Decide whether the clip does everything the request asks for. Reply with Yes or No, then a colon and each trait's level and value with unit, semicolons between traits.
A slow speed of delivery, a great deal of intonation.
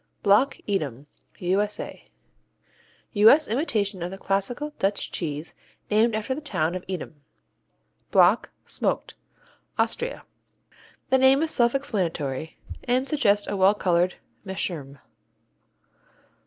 Yes: slow, 110 wpm; wide, 5.9 semitones